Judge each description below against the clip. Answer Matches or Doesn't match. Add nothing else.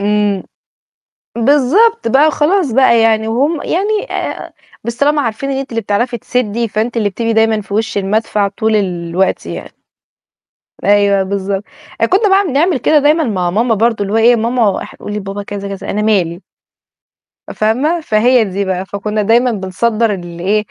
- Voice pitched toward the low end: Doesn't match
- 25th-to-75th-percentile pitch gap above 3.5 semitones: Matches